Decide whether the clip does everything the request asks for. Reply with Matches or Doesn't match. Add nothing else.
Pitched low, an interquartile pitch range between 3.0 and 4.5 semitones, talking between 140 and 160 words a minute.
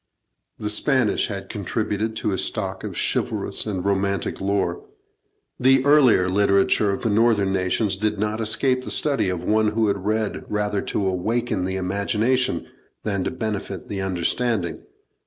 Doesn't match